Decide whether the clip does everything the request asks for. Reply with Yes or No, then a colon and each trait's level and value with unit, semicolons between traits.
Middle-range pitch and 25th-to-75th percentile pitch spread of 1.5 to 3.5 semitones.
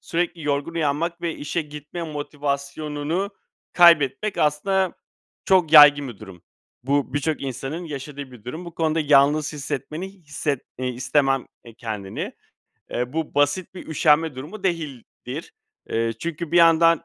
Yes: medium, 150 Hz; average, 3.1 semitones